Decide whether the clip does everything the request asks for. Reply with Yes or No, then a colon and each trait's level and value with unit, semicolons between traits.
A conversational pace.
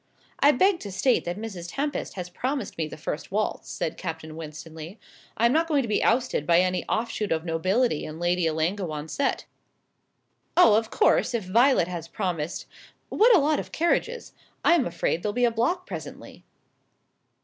Yes: average, 180 wpm